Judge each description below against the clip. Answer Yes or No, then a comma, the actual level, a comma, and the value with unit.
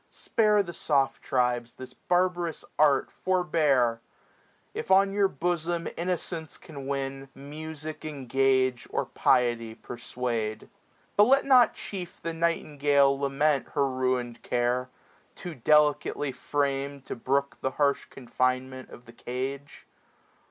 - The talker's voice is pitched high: No, medium, 140 Hz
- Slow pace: Yes, slow, 125 wpm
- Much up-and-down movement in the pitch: No, average, 4.3 semitones